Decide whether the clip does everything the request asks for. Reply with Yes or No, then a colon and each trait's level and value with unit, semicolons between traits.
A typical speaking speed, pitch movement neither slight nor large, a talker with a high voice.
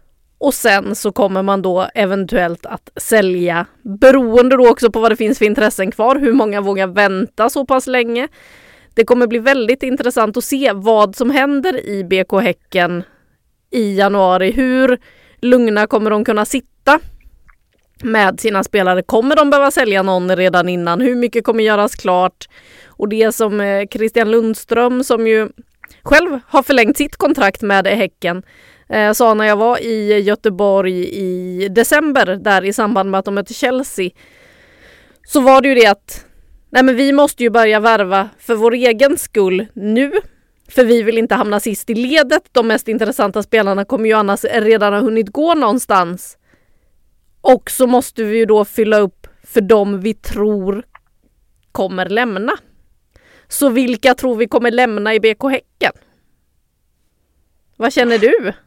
Yes: average, 160 wpm; average, 3.8 semitones; high, 225 Hz